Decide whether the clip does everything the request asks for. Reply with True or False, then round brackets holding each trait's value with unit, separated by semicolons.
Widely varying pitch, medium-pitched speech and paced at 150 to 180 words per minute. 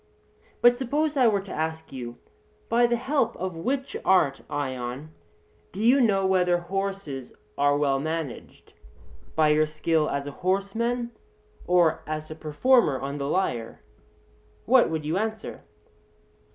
False (7.1 semitones; 175 Hz; 140 wpm)